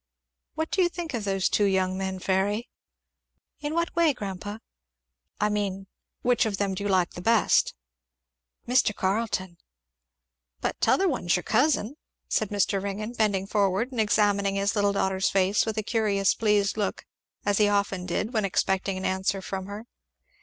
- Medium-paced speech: Yes, average, 165 wpm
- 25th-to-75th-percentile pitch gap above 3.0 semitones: No, narrow, 2.4 semitones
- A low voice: No, high, 205 Hz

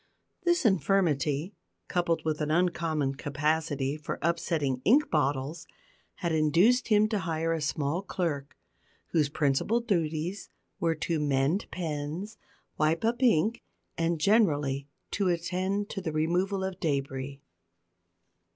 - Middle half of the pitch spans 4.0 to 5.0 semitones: Yes, average, 4.4 semitones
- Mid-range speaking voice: Yes, medium, 165 Hz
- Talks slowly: Yes, slow, 125 wpm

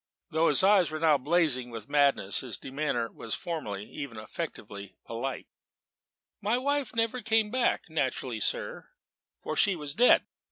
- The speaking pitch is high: No, medium, 150 Hz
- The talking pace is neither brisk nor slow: Yes, average, 150 wpm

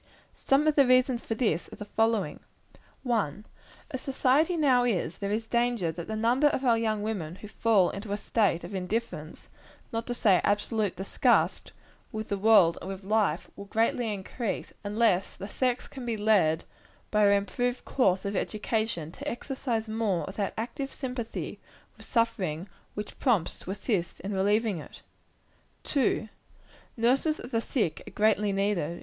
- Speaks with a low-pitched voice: No, high, 215 Hz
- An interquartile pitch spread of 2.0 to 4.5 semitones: Yes, average, 3.5 semitones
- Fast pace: No, average, 165 wpm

